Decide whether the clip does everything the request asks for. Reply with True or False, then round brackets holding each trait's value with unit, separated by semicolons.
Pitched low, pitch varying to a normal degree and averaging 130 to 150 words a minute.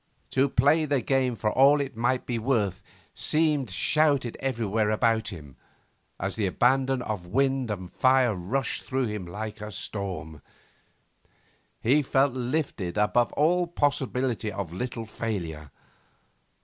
True (120 Hz; 4.5 semitones; 135 wpm)